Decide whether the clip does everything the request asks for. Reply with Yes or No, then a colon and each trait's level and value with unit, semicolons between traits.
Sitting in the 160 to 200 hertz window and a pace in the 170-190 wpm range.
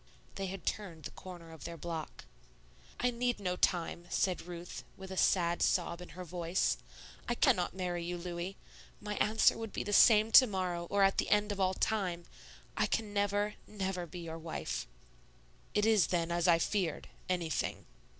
Yes: medium, 185 Hz; average, 180 wpm